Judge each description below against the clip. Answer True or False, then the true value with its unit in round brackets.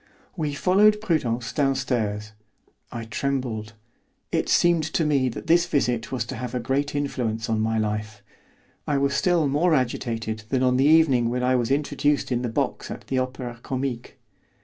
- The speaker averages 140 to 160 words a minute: False (170 wpm)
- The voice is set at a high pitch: False (130 Hz)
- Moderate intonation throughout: True (3.9 semitones)